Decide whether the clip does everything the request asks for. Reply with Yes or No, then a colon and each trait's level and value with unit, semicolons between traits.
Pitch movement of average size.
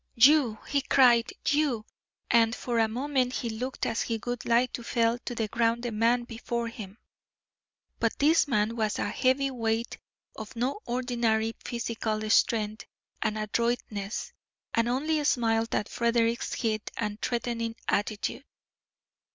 No: narrow, 1.8 semitones